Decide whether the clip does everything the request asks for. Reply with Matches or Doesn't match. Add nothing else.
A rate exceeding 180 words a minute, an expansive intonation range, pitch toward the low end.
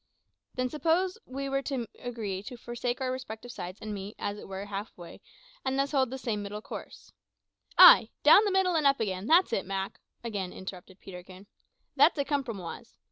Doesn't match